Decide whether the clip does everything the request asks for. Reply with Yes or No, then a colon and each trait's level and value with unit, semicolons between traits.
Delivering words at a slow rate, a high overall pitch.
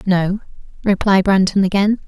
Yes: slow, 115 wpm; high, 195 Hz